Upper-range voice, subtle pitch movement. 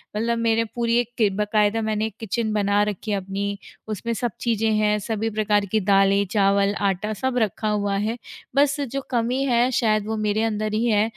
Yes: high, 215 Hz; narrow, 2.0 semitones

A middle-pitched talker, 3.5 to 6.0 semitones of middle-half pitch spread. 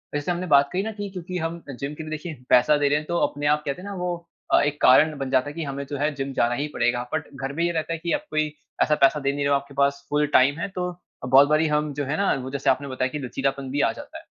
No: medium, 145 Hz; average, 2.8 semitones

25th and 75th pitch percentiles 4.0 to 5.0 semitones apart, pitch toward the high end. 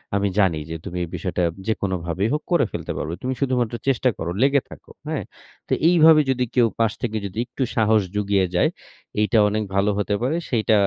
No: average, 4.6 semitones; low, 110 Hz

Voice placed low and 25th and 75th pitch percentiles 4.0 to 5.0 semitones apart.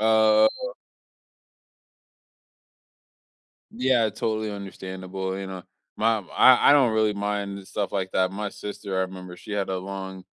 No: low, 100 Hz; narrow, 2.4 semitones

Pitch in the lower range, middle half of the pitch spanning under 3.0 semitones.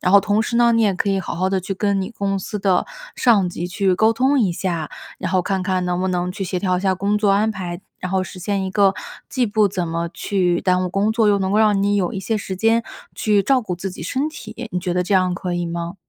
No: high, 195 Hz; narrow, 2.5 semitones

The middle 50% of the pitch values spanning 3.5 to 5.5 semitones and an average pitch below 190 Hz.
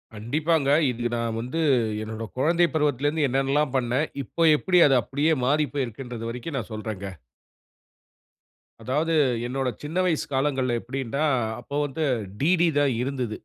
Yes: average, 3.8 semitones; low, 135 Hz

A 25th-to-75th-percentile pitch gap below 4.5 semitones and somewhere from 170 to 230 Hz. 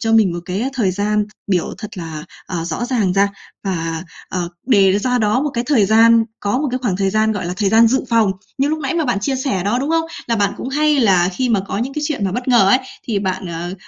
No: average, 4.8 semitones; high, 215 Hz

